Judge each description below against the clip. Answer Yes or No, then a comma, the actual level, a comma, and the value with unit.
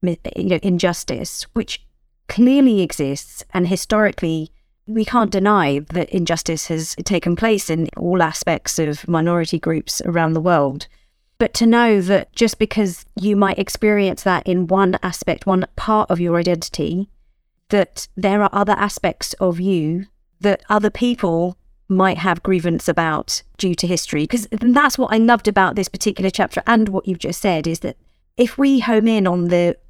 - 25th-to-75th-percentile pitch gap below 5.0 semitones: Yes, average, 3.5 semitones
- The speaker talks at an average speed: Yes, average, 165 wpm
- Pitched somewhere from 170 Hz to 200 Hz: Yes, high, 190 Hz